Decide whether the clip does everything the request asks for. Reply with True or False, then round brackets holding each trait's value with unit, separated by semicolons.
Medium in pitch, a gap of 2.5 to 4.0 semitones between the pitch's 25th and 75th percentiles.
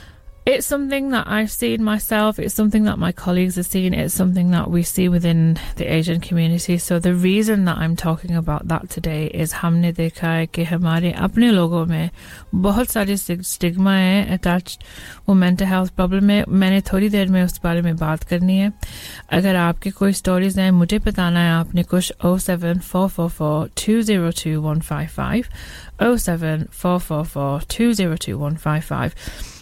True (180 Hz; 2.8 semitones)